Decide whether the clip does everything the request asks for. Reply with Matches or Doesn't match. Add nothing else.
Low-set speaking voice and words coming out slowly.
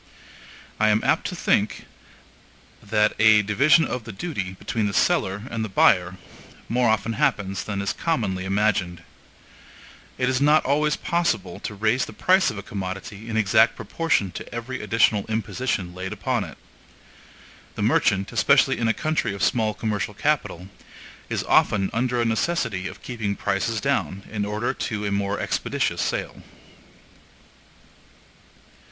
Doesn't match